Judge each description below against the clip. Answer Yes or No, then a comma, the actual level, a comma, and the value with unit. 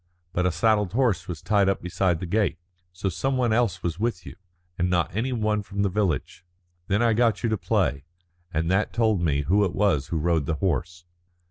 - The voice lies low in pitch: Yes, very low, 95 Hz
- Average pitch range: Yes, average, 3.8 semitones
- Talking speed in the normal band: No, fast, 215 wpm